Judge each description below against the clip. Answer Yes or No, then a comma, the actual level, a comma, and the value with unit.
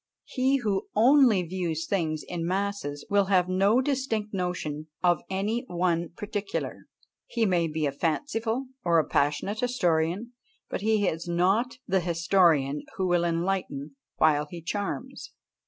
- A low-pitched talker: No, medium, 185 Hz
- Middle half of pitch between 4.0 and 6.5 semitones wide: Yes, average, 4.4 semitones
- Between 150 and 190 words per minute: No, average, 140 wpm